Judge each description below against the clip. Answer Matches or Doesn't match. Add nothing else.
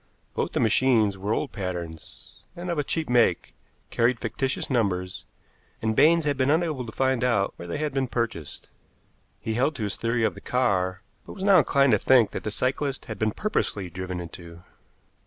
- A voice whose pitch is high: Doesn't match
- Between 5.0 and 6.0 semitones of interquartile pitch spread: Matches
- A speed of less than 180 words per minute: Doesn't match